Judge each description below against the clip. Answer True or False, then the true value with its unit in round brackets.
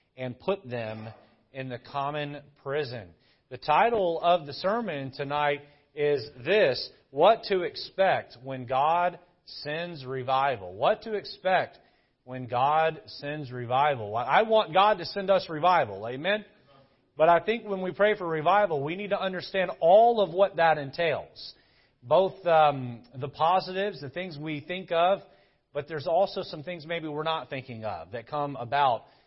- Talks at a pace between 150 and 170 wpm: True (155 wpm)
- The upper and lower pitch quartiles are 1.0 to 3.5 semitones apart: False (5.6 semitones)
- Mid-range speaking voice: True (155 Hz)